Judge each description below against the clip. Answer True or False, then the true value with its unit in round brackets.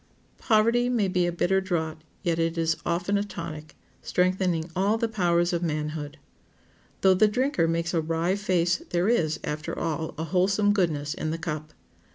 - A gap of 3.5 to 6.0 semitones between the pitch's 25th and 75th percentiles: False (3.0 semitones)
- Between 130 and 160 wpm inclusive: False (175 wpm)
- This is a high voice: False (175 Hz)